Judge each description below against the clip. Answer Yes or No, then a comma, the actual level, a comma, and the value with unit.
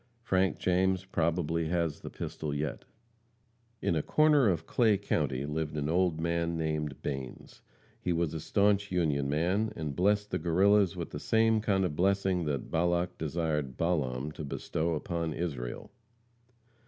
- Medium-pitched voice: No, very low, 85 Hz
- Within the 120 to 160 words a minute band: Yes, average, 155 wpm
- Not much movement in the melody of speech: No, average, 3.8 semitones